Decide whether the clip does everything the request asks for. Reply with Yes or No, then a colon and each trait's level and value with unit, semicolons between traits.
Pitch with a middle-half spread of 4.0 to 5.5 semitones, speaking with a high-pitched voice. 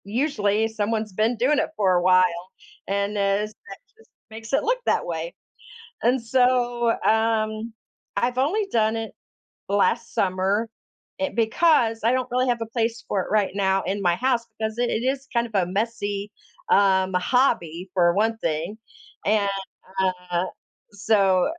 No: average, 3.3 semitones; high, 220 Hz